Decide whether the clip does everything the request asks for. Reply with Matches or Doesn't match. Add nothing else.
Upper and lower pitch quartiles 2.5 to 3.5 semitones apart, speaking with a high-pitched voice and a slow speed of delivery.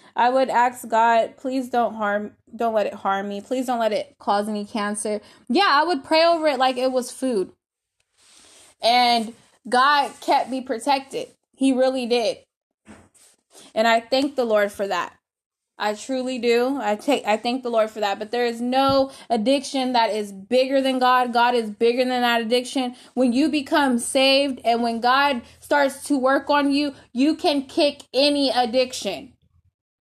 Doesn't match